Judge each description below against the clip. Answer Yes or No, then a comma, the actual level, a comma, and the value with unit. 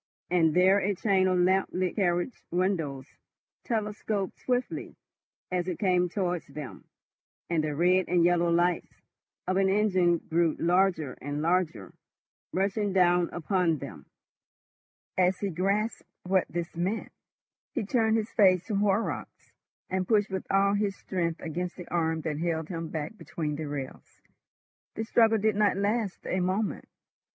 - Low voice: No, medium, 185 Hz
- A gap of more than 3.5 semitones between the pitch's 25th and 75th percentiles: No, average, 2.9 semitones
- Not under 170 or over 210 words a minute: No, average, 150 wpm